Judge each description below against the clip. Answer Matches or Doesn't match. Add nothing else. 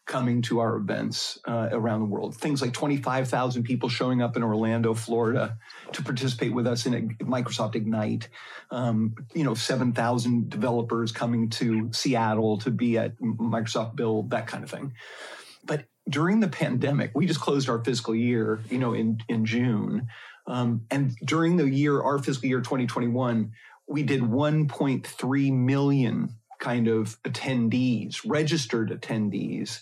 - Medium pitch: Doesn't match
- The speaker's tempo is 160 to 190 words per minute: Doesn't match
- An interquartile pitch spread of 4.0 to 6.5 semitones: Doesn't match